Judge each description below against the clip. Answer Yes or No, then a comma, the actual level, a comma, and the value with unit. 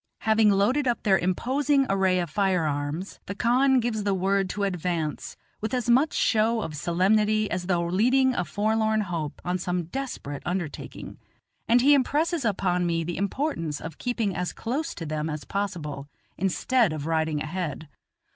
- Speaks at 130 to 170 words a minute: Yes, average, 165 wpm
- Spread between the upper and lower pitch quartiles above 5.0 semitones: Yes, wide, 5.4 semitones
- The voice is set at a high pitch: Yes, high, 195 Hz